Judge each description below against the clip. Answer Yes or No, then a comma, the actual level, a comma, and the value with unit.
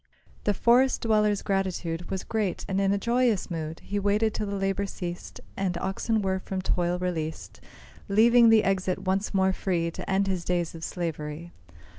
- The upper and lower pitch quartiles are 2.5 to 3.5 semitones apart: Yes, average, 2.8 semitones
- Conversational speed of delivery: Yes, average, 175 wpm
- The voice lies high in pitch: Yes, high, 195 Hz